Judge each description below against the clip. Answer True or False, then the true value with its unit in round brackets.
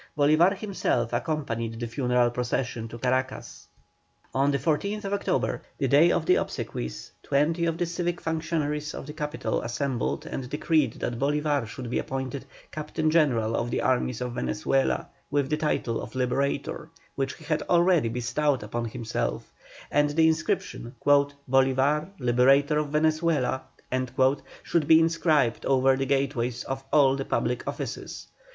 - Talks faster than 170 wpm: False (150 wpm)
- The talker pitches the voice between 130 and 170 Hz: True (140 Hz)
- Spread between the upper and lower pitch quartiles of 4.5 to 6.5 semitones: False (3.8 semitones)